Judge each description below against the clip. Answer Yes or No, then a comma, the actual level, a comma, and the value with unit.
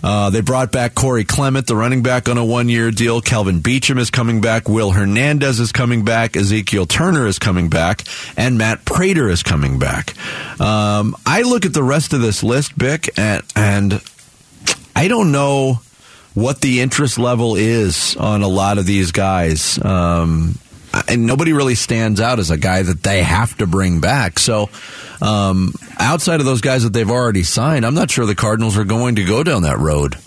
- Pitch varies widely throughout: No, average, 4.2 semitones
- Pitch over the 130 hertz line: No, low, 115 Hz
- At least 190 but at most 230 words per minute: Yes, average, 195 wpm